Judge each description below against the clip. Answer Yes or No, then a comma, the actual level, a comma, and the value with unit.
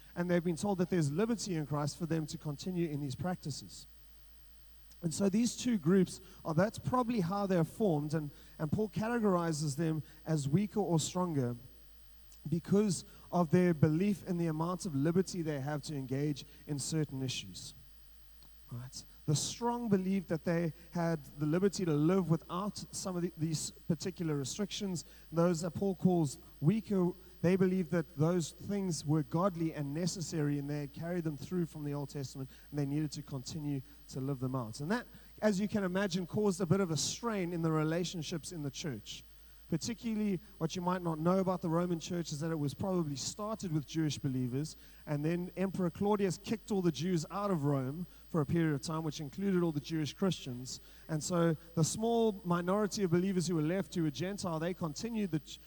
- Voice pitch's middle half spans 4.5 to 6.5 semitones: No, average, 3.8 semitones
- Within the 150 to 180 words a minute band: No, average, 190 wpm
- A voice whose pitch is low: No, medium, 170 Hz